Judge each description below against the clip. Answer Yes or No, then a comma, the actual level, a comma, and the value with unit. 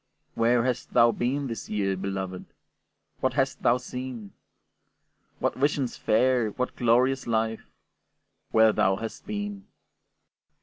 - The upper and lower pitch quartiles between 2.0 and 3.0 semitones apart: Yes, average, 2.7 semitones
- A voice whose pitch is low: Yes, low, 120 Hz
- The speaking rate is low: Yes, slow, 120 wpm